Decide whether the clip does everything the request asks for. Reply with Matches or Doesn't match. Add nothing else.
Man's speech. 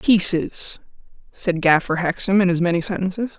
Doesn't match